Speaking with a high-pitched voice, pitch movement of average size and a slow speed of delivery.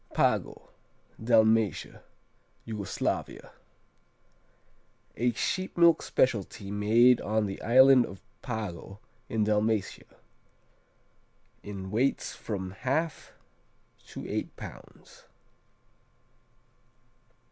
No: low, 110 Hz; average, 3.4 semitones; slow, 75 wpm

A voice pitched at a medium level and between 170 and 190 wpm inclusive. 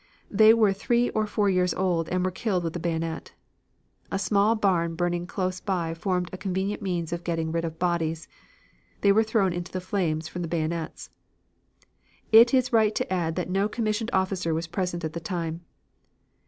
Yes: medium, 180 Hz; average, 185 wpm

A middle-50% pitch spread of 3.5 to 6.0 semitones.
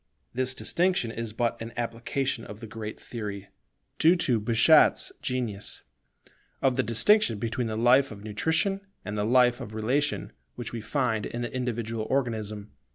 No: average, 2.9 semitones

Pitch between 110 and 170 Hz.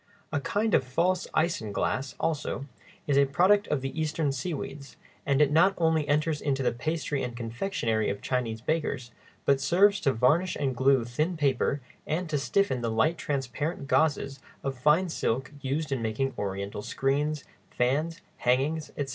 Yes: medium, 140 Hz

